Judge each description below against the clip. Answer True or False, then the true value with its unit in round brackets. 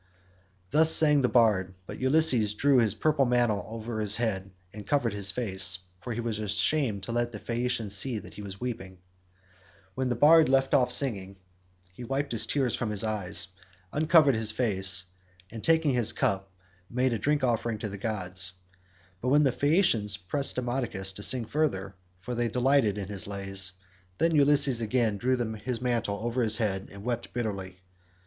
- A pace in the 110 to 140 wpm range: False (180 wpm)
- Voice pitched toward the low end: True (115 Hz)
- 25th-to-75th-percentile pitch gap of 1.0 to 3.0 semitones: False (4.4 semitones)